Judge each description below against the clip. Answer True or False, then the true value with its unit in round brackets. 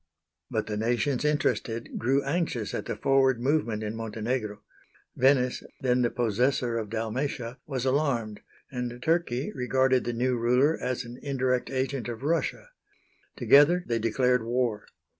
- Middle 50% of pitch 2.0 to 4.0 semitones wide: True (2.7 semitones)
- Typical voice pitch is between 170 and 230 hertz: False (125 Hz)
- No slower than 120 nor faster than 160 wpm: True (140 wpm)